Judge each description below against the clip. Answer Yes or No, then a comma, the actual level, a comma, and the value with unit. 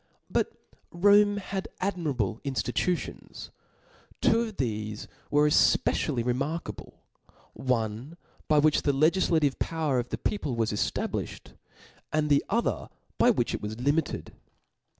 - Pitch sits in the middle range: Yes, medium, 150 Hz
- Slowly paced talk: Yes, slow, 125 wpm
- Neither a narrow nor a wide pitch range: No, wide, 5.9 semitones